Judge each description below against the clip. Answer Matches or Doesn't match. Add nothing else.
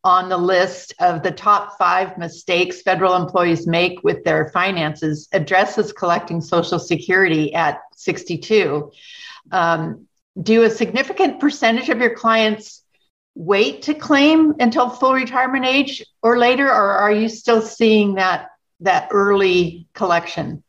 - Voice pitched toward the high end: Matches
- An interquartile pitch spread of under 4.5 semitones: Doesn't match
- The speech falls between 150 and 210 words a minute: Doesn't match